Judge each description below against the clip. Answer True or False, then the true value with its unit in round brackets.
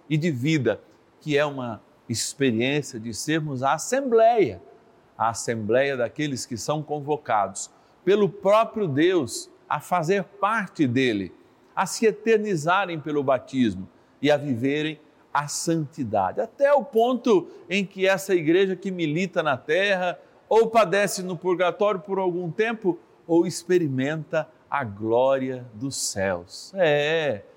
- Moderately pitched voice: True (170 Hz)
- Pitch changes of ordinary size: False (5.9 semitones)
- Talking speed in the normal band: True (130 wpm)